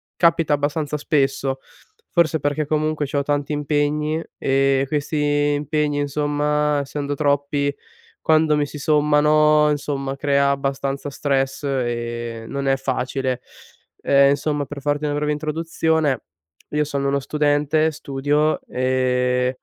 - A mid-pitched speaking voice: Yes, medium, 145 Hz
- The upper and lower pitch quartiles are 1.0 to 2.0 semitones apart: Yes, narrow, 1.6 semitones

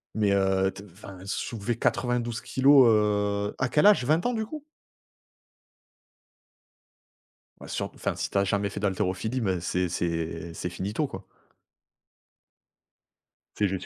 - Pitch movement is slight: No, average, 4.7 semitones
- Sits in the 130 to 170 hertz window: No, low, 100 Hz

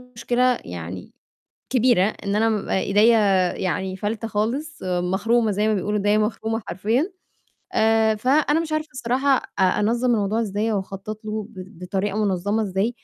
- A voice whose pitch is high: Yes, high, 215 Hz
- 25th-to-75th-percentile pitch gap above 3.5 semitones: No, average, 3.1 semitones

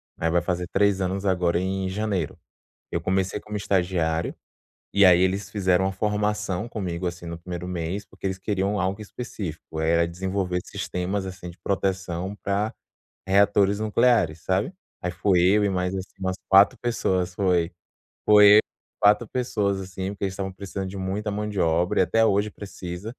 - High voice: No, very low, 95 Hz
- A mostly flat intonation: Yes, narrow, 2.2 semitones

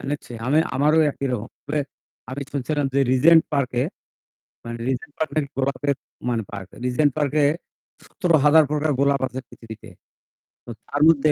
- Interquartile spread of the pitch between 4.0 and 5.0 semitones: No, average, 2.9 semitones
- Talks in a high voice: No, medium, 140 Hz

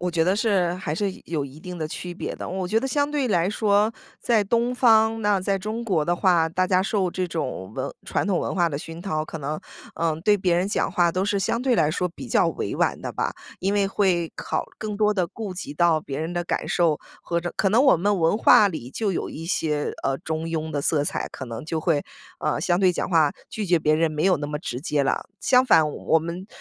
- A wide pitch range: No, average, 4.1 semitones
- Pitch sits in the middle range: Yes, medium, 180 Hz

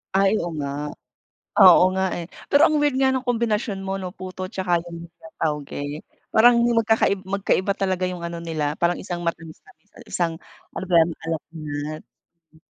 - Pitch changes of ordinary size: Yes, average, 3.4 semitones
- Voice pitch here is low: No, medium, 180 Hz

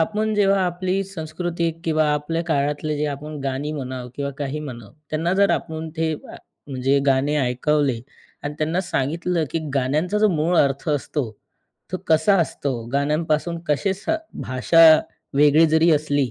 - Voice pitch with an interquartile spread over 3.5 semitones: No, average, 3.1 semitones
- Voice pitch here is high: No, medium, 155 Hz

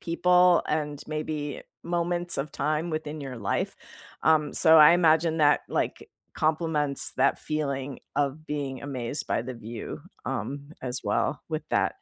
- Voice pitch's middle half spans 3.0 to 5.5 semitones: No, narrow, 2.4 semitones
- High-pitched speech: No, medium, 150 Hz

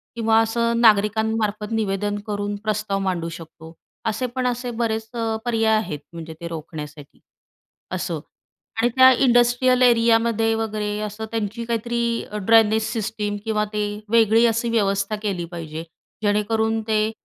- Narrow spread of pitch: Yes, narrow, 1.9 semitones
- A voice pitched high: Yes, high, 220 Hz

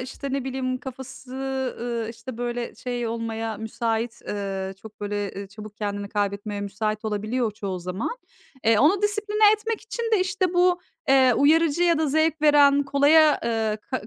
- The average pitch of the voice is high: Yes, high, 245 Hz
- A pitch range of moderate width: No, wide, 5.9 semitones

